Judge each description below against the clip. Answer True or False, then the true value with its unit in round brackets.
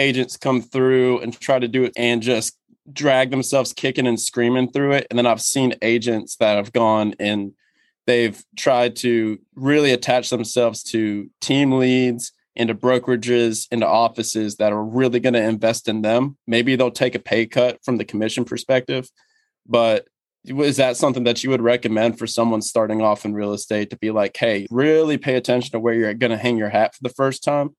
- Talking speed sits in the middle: True (195 wpm)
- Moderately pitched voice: False (120 Hz)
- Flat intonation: True (2.3 semitones)